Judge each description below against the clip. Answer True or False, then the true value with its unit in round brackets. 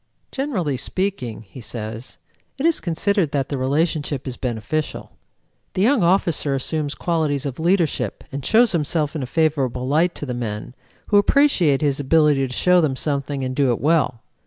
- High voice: False (145 Hz)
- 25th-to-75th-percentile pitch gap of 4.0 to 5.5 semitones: True (4.6 semitones)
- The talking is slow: False (170 wpm)